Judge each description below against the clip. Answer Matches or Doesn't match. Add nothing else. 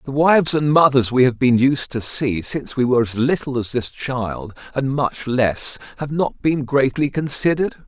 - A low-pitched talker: Matches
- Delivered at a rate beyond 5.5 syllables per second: Doesn't match